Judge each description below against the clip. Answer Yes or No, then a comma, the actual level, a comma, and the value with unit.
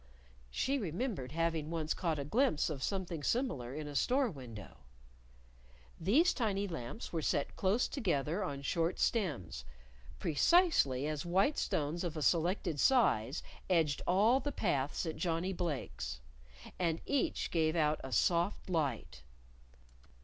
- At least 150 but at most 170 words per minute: No, slow, 135 wpm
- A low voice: No, medium, 165 Hz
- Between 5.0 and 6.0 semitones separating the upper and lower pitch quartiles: Yes, average, 5.3 semitones